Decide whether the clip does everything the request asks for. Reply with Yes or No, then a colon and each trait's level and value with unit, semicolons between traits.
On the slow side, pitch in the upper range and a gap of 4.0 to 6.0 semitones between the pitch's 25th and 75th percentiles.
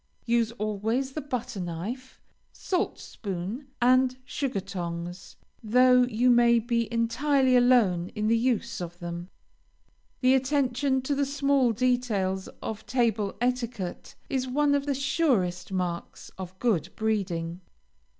Yes: slow, 130 wpm; high, 235 Hz; average, 5.1 semitones